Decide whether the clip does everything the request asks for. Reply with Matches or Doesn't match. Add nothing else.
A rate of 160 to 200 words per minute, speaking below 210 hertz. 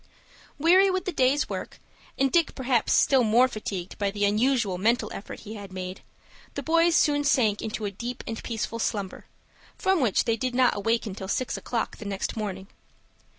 Doesn't match